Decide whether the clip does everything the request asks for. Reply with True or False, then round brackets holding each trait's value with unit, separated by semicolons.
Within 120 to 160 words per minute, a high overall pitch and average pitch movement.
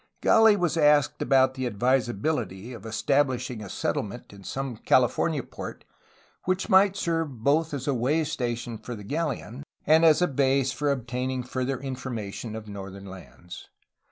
False (155 wpm; 130 Hz; 4.4 semitones)